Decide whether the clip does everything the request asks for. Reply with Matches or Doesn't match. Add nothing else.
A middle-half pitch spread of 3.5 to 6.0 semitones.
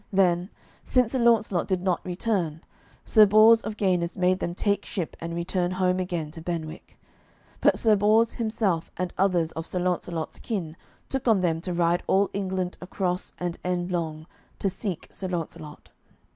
Doesn't match